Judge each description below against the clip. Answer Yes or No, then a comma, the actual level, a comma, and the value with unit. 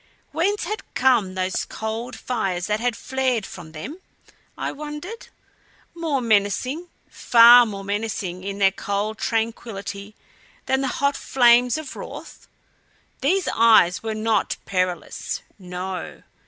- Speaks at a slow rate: Yes, slow, 125 wpm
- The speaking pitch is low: No, high, 225 Hz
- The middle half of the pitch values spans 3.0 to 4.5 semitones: No, average, 5.0 semitones